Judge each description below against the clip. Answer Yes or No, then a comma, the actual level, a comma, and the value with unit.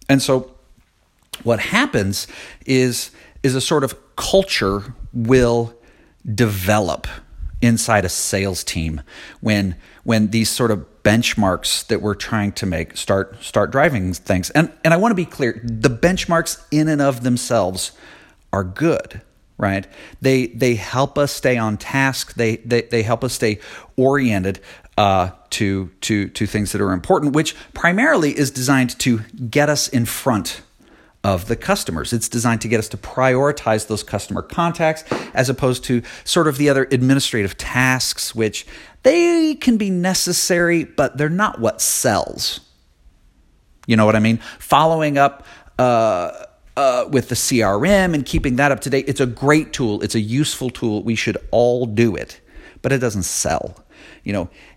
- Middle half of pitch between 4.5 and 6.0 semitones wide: Yes, wide, 5.4 semitones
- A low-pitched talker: Yes, low, 120 Hz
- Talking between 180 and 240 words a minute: No, average, 160 wpm